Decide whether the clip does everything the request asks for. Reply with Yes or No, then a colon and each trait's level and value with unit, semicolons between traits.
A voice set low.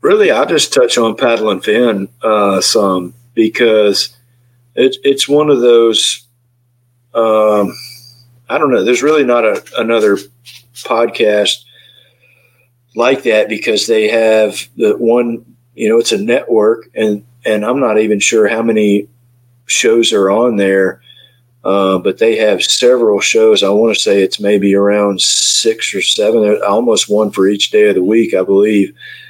Yes: low, 120 Hz